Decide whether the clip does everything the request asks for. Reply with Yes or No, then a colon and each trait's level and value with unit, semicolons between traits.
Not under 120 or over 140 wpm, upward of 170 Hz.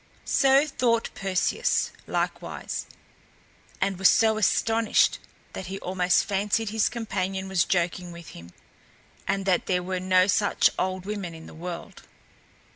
Yes: slow, 135 wpm; high, 190 Hz